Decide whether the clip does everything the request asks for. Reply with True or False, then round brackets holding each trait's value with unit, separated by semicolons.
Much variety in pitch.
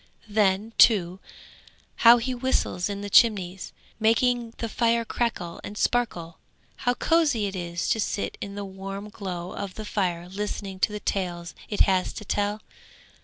False (3.5 semitones)